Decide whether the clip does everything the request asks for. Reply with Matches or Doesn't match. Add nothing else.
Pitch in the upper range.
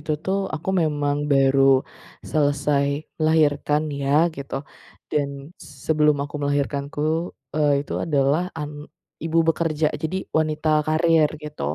Doesn't match